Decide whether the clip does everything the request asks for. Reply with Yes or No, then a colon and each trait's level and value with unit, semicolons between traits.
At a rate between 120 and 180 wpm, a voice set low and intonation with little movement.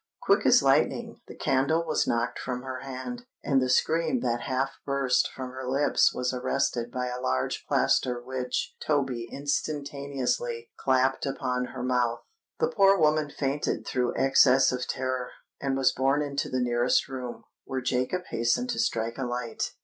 Yes: average, 165 wpm; low, 130 Hz; narrow, 2.1 semitones